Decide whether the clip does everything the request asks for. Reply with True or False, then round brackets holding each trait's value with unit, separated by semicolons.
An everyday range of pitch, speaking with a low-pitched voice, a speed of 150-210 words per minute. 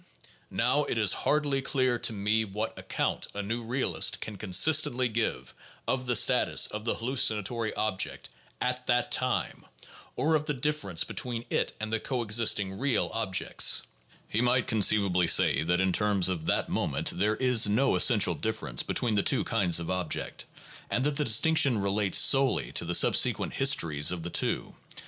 True (4.4 semitones; 110 Hz; 170 wpm)